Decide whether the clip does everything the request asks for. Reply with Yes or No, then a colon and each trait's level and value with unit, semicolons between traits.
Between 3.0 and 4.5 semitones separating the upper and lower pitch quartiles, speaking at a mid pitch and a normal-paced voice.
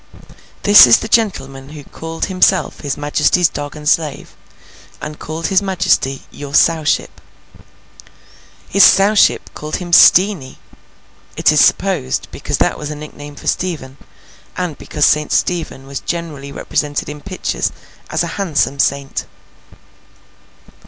No: average, 4.0 semitones; medium, 150 Hz; slow, 130 wpm